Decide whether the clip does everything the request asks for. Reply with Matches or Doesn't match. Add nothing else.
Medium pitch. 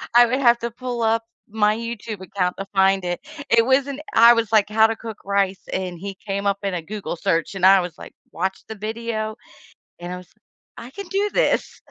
Doesn't match